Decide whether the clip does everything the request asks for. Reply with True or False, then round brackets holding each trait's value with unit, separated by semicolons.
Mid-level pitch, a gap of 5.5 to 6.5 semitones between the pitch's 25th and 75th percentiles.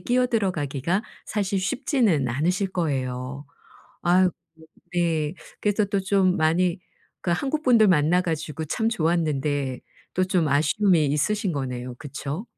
False (175 Hz; 5.1 semitones)